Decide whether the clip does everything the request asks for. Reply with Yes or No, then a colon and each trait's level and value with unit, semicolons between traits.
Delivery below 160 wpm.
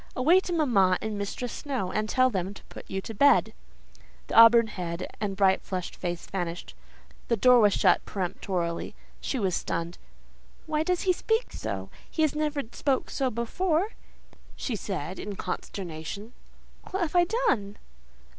Yes: average, 150 wpm